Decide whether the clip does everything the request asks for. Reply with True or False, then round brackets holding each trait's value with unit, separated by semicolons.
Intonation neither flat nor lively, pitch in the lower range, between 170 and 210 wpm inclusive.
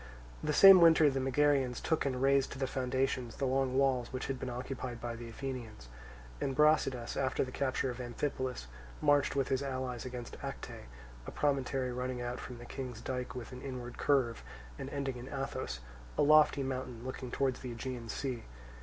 False (1.7 semitones; 130 Hz; 185 wpm)